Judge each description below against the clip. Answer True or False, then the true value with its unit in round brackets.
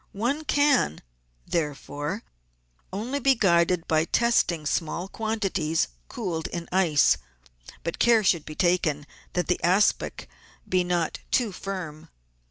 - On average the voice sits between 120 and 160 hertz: False (180 Hz)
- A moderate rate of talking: False (120 wpm)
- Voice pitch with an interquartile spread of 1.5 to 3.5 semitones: False (5.0 semitones)